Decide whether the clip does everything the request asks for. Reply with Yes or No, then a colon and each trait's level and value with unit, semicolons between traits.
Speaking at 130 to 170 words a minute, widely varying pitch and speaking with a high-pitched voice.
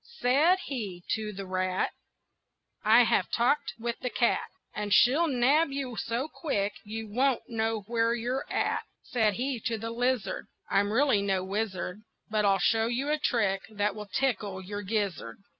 No: average, 165 wpm; average, 3.7 semitones; high, 225 Hz